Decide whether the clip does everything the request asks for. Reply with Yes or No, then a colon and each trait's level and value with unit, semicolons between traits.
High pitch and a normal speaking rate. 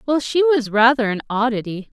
Yes: high, 245 Hz; average, 180 wpm